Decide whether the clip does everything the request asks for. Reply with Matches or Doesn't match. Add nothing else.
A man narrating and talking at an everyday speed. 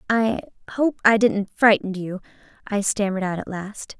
Doesn't match